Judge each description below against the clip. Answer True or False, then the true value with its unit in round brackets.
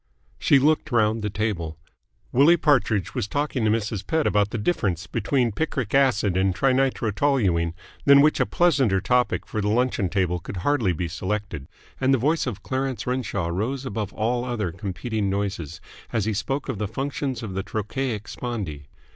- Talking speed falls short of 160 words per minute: False (170 wpm)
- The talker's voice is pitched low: True (110 Hz)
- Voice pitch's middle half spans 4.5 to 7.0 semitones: True (5.2 semitones)